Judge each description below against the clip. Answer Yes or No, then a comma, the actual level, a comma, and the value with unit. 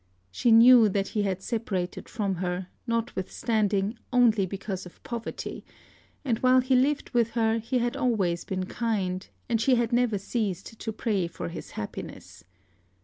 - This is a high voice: Yes, high, 220 Hz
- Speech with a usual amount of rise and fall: Yes, average, 3.8 semitones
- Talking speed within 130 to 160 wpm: Yes, average, 155 wpm